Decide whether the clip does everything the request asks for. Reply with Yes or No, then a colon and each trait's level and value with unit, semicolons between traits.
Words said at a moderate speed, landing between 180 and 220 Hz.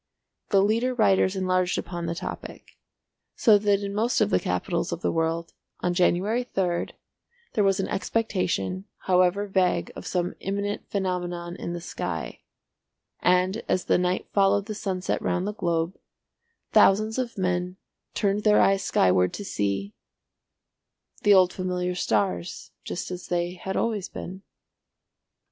Yes: average, 145 wpm; medium, 185 Hz